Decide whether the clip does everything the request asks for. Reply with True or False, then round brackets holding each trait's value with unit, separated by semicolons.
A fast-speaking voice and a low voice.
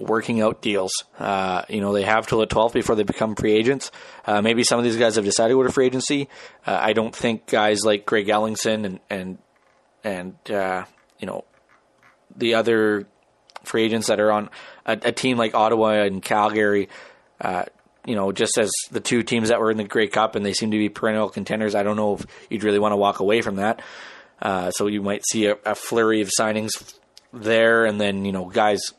True (215 wpm; 110 Hz)